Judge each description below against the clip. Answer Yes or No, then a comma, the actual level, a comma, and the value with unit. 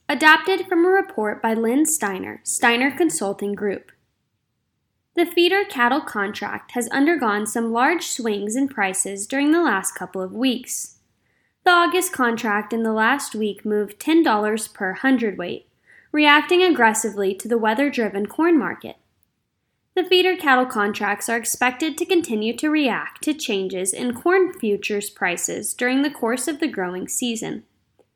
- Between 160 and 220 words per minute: No, average, 145 wpm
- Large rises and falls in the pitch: Yes, wide, 6.8 semitones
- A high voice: Yes, high, 245 Hz